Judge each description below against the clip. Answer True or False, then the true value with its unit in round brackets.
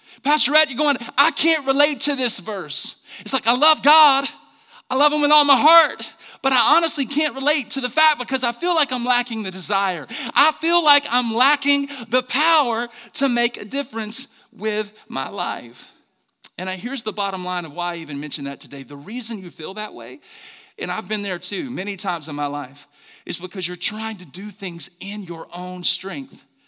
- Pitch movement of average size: False (7.3 semitones)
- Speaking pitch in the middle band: False (235 Hz)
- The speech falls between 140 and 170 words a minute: False (205 wpm)